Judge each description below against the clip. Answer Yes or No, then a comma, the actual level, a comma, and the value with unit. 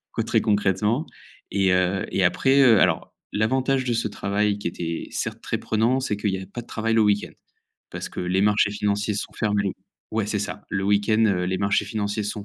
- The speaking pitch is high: No, low, 105 Hz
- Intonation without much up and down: Yes, narrow, 2.0 semitones